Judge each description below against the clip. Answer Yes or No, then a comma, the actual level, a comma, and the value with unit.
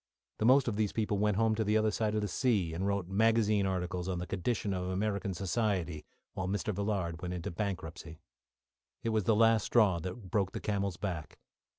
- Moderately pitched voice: No, low, 100 Hz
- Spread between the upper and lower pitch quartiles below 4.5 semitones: Yes, average, 3.0 semitones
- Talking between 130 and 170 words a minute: No, fast, 205 wpm